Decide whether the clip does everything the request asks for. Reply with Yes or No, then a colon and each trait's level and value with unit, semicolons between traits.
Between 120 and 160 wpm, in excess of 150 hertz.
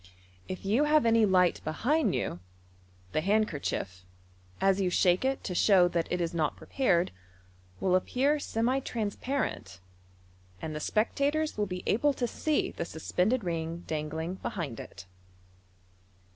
Yes: average, 145 wpm; high, 190 Hz